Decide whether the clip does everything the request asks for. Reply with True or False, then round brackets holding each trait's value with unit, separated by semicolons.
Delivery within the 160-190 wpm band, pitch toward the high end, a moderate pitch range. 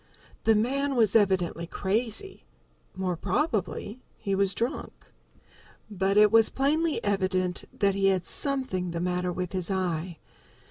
False (135 wpm; 195 Hz; 3.8 semitones)